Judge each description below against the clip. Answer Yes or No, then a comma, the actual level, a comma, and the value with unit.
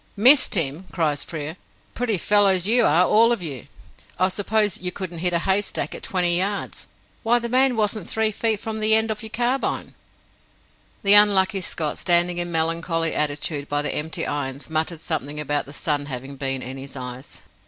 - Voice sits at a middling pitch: Yes, medium, 175 Hz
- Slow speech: No, average, 185 wpm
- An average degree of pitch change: No, wide, 6.0 semitones